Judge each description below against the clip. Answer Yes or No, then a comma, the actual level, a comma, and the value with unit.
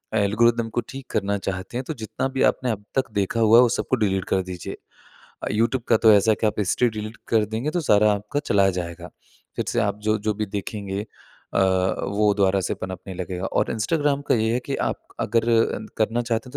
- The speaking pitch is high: No, low, 110 Hz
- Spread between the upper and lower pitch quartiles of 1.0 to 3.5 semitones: Yes, average, 2.8 semitones